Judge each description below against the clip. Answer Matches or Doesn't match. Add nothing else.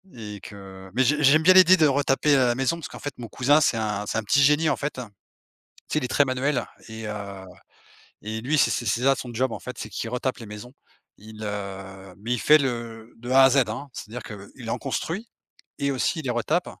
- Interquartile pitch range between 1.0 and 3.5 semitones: Doesn't match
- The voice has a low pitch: Matches